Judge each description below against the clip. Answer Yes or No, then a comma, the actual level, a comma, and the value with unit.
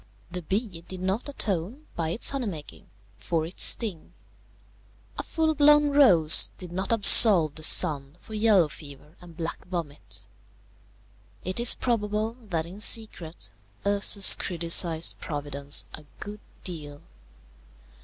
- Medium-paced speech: No, slow, 130 wpm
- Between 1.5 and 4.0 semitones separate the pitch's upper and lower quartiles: No, average, 5.2 semitones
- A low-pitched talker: No, medium, 180 Hz